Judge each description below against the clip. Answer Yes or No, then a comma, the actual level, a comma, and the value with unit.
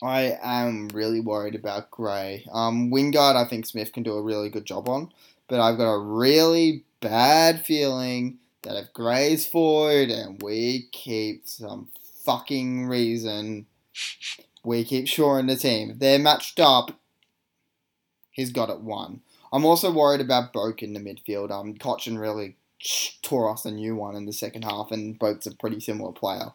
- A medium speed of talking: Yes, average, 165 wpm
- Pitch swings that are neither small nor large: Yes, average, 3.7 semitones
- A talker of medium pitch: No, low, 115 Hz